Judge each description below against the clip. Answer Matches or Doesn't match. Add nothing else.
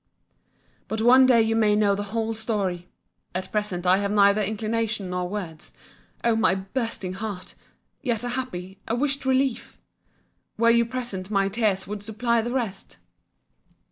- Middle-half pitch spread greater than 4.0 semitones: Doesn't match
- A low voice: Doesn't match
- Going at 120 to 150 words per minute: Matches